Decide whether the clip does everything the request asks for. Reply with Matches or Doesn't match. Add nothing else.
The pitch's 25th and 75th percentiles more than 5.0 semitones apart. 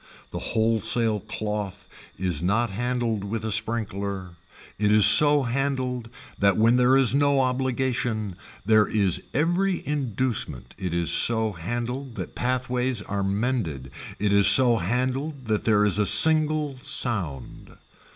Doesn't match